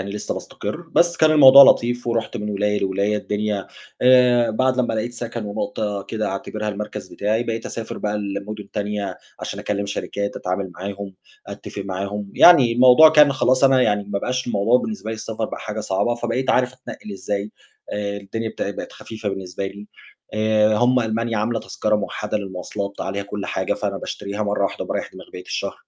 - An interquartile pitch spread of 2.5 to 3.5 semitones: Yes, average, 2.9 semitones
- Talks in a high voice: No, low, 105 Hz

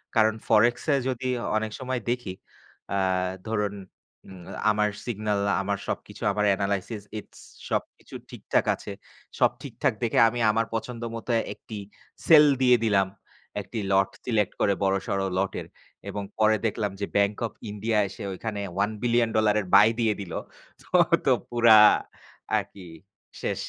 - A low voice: Yes, low, 105 Hz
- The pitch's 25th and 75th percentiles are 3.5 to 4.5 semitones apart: No, narrow, 2.4 semitones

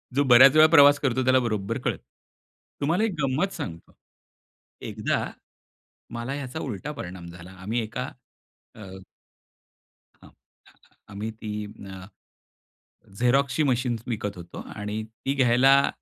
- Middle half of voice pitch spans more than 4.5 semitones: Yes, average, 5.0 semitones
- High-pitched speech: No, low, 120 Hz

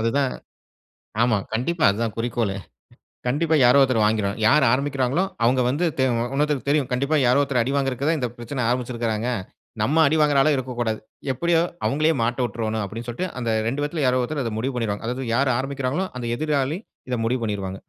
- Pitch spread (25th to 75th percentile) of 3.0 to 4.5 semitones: Yes, average, 3.5 semitones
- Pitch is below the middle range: Yes, low, 125 Hz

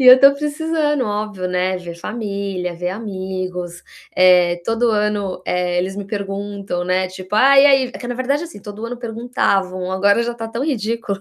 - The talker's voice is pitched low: No, high, 205 Hz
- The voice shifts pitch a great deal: No, average, 4.5 semitones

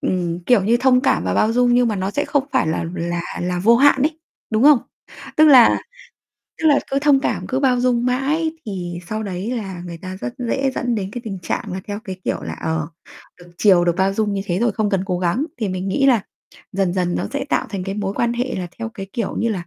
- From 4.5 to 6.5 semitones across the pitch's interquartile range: Yes, average, 5.2 semitones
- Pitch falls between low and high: No, high, 215 Hz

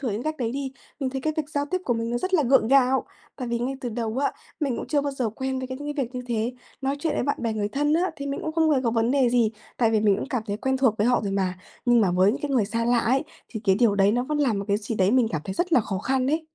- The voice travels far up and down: No, average, 3.9 semitones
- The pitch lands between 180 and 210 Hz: No, very high, 250 Hz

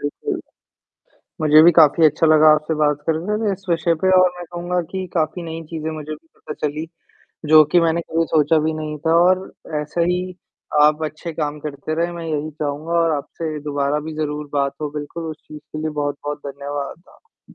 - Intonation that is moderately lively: No, narrow, 1.9 semitones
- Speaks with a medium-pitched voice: Yes, medium, 155 Hz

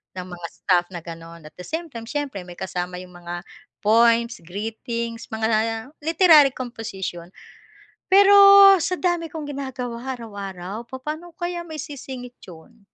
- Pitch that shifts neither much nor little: No, wide, 7.7 semitones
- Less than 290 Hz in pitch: Yes, high, 230 Hz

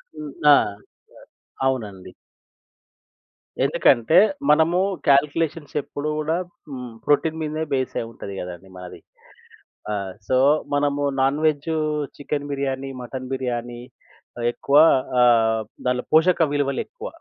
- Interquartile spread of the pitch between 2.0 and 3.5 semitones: No, average, 4.0 semitones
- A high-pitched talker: No, medium, 140 Hz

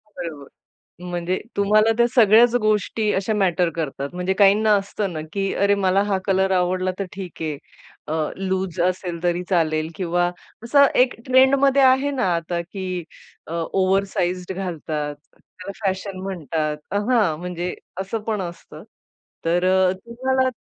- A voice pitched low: No, high, 190 Hz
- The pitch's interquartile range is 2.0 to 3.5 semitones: Yes, average, 3.1 semitones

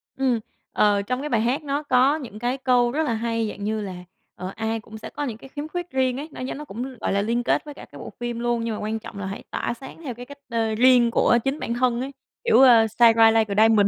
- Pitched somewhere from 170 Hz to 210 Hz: No, high, 240 Hz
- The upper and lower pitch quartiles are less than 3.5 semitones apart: Yes, average, 3.1 semitones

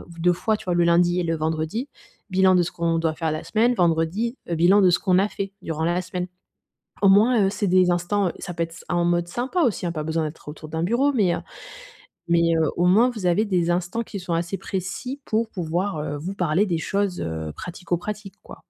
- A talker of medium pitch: Yes, medium, 180 Hz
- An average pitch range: Yes, average, 3.2 semitones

